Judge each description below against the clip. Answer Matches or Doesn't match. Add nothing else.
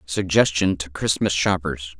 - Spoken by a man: Matches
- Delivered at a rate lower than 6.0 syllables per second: Matches